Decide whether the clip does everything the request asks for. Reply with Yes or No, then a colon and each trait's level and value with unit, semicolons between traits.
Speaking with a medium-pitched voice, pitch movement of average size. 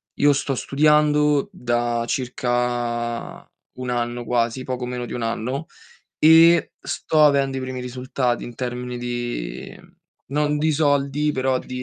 No: low, 125 Hz; average, 3.0 semitones